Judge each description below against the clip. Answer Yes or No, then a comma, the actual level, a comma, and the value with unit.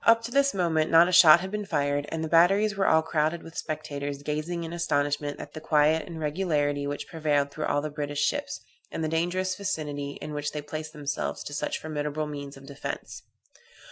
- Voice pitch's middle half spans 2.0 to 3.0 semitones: Yes, average, 2.7 semitones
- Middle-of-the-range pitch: Yes, medium, 155 Hz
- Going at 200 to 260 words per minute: Yes, fast, 205 wpm